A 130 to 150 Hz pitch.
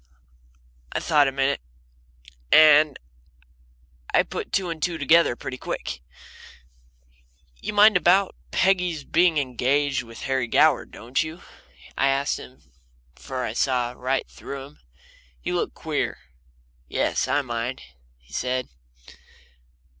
Yes: medium, 140 Hz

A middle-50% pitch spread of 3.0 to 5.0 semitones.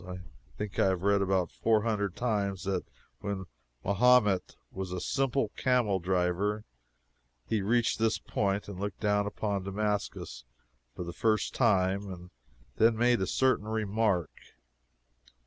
No: narrow, 2.6 semitones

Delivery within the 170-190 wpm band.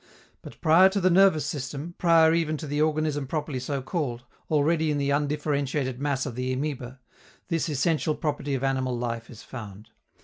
Yes: average, 175 wpm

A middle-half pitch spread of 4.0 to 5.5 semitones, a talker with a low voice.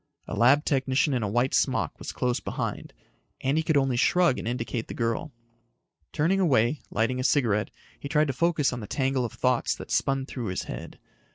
No: average, 3.4 semitones; low, 130 Hz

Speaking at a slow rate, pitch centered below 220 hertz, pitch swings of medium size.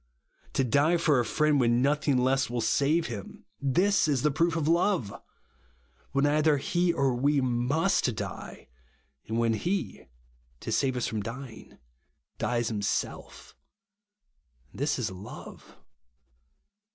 Yes: slow, 130 wpm; low, 135 Hz; average, 4.3 semitones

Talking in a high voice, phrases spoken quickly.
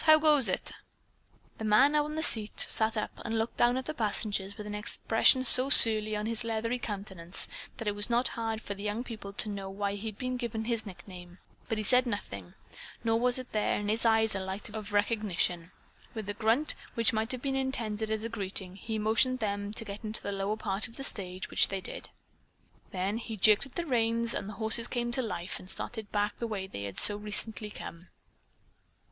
Yes: high, 215 Hz; fast, 215 wpm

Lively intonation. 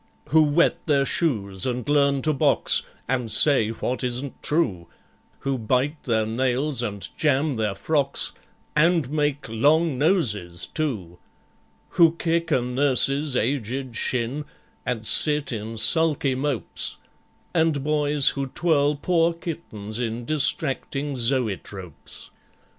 No: average, 4.5 semitones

